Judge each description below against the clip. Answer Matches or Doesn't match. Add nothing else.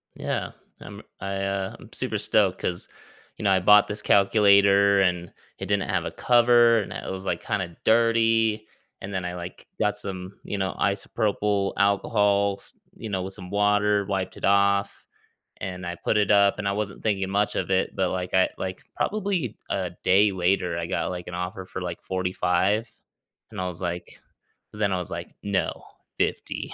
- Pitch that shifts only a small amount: Matches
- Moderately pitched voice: Doesn't match